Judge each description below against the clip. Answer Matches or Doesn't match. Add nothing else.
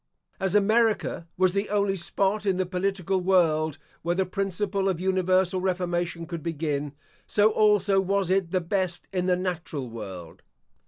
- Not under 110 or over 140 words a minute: Doesn't match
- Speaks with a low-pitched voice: Doesn't match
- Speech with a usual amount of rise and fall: Doesn't match